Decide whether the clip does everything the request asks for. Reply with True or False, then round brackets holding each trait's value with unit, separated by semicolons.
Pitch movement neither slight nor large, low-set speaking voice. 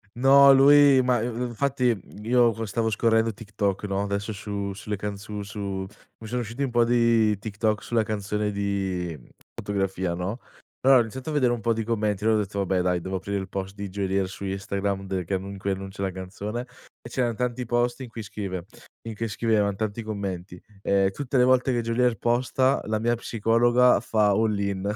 True (3.3 semitones; 105 Hz)